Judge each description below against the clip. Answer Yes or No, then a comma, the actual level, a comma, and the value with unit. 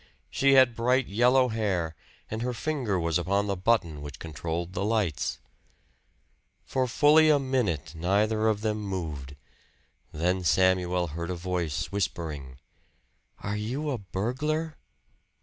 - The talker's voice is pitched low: Yes, low, 100 Hz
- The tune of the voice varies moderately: No, wide, 6.2 semitones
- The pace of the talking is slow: Yes, slow, 130 wpm